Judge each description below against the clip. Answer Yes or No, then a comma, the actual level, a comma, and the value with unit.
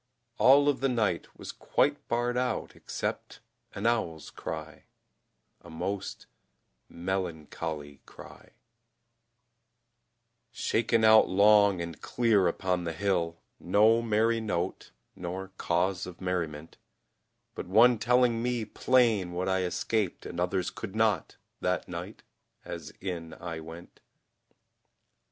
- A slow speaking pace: Yes, slow, 115 wpm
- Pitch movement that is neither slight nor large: Yes, average, 4.7 semitones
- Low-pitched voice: Yes, very low, 95 Hz